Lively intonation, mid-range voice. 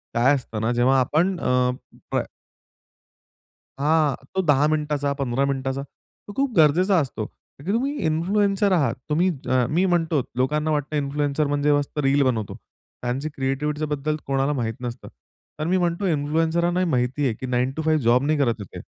No: average, 3.4 semitones; medium, 145 Hz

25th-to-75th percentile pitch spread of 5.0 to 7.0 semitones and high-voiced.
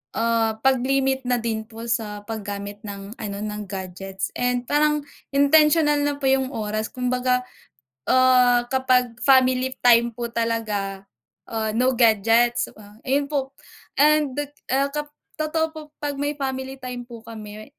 No: average, 3.6 semitones; high, 245 Hz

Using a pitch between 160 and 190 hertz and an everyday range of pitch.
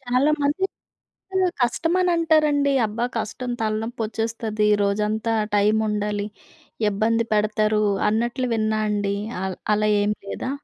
No: high, 220 Hz; average, 3.2 semitones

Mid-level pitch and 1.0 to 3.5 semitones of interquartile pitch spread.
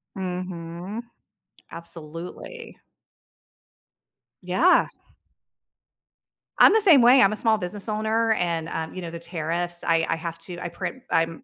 No: medium, 180 Hz; average, 4.6 semitones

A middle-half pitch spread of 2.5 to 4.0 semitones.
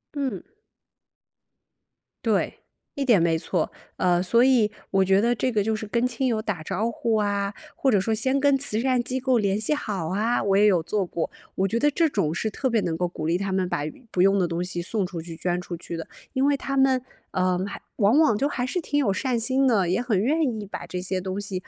No: wide, 5.4 semitones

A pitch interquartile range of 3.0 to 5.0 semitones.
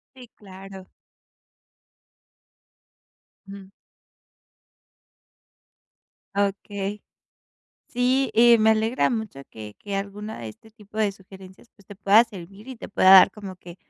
No: narrow, 2.4 semitones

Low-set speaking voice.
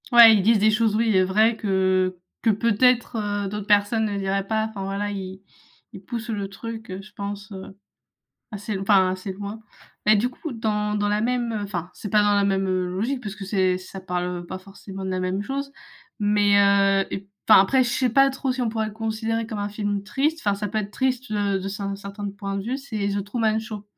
No: high, 205 Hz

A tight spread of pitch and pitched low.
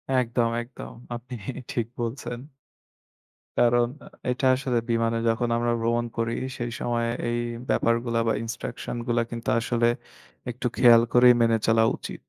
Yes: narrow, 0.8 semitones; low, 120 Hz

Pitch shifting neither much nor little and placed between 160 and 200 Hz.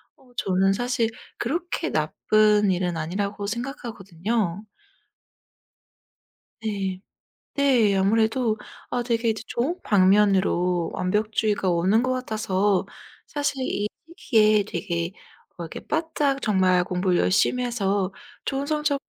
No: average, 4.4 semitones; high, 210 Hz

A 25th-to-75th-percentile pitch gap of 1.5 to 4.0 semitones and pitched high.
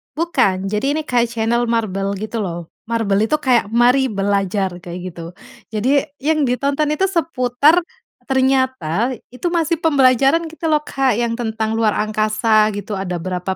No: average, 5.1 semitones; high, 235 Hz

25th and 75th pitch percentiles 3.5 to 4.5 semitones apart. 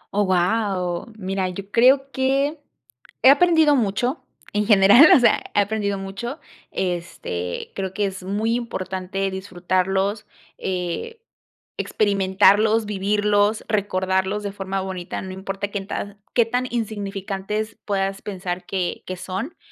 No: narrow, 2.6 semitones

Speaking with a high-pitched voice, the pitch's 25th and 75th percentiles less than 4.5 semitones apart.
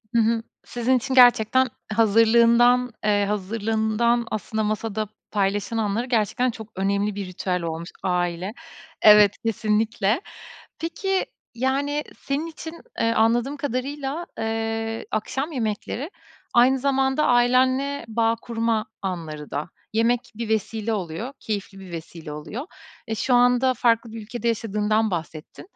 Yes: high, 225 Hz; average, 3.1 semitones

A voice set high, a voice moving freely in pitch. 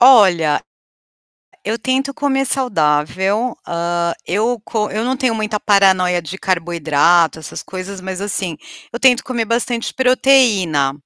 Yes: high, 200 Hz; wide, 6.0 semitones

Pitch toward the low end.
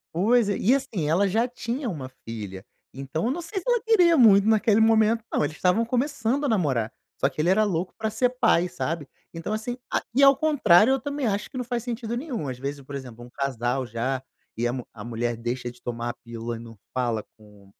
No: medium, 185 Hz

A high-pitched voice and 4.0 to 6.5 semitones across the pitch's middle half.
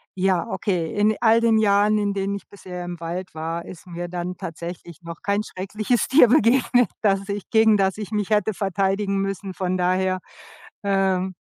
No: high, 195 Hz; narrow, 2.6 semitones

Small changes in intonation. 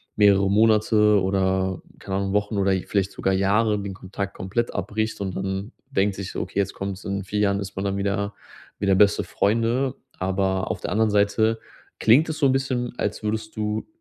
Yes: narrow, 2.0 semitones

